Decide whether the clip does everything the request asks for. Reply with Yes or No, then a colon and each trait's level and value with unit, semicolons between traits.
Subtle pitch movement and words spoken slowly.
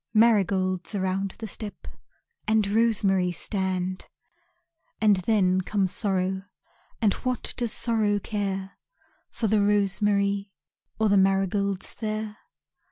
Yes: narrow, 2.1 semitones; slow, 105 wpm